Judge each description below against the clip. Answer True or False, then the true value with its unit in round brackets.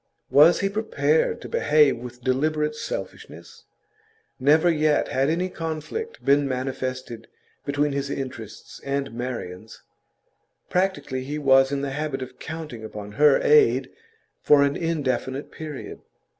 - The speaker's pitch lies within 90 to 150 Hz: True (140 Hz)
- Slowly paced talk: True (130 wpm)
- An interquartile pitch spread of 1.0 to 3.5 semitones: True (3.0 semitones)